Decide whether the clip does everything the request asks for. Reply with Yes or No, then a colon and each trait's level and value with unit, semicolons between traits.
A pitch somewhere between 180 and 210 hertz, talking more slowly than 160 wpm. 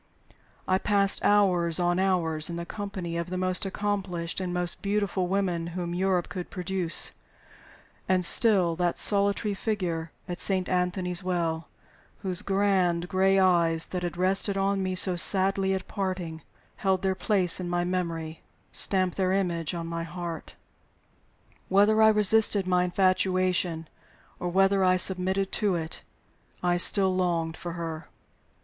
Yes: medium, 185 Hz; average, 145 wpm